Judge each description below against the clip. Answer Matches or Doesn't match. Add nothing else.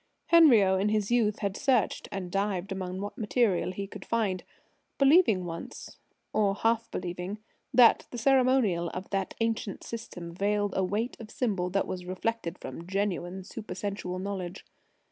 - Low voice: Doesn't match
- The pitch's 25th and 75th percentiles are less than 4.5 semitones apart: Matches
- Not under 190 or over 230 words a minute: Doesn't match